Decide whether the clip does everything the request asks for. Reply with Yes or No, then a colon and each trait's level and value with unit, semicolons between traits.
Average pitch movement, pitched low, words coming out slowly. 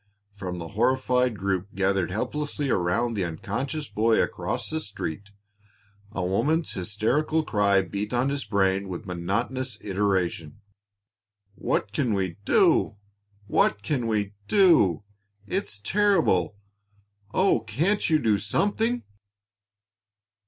No: wide, 6.2 semitones; low, 105 Hz; slow, 115 wpm